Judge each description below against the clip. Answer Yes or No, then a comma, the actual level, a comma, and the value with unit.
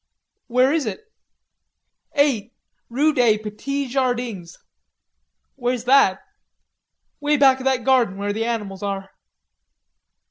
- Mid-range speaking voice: No, high, 245 Hz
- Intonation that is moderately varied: Yes, average, 4.1 semitones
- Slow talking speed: Yes, slow, 110 wpm